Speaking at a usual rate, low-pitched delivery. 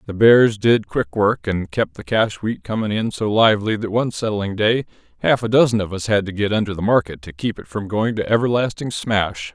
No: fast, 235 wpm; low, 105 Hz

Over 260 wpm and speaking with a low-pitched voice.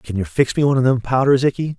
Yes: fast, 305 wpm; low, 125 Hz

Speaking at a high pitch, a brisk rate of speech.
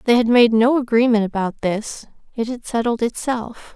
No: high, 230 Hz; average, 175 wpm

